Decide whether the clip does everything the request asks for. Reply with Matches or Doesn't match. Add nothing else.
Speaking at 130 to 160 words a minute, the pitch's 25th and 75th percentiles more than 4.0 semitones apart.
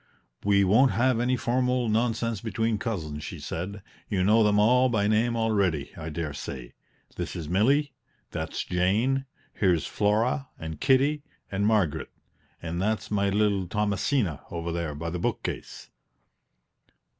Matches